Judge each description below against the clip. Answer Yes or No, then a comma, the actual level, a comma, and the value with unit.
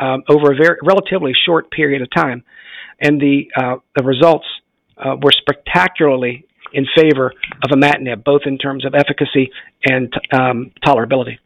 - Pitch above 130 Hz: Yes, medium, 140 Hz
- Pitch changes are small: Yes, narrow, 2.1 semitones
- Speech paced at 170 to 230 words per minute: No, average, 155 wpm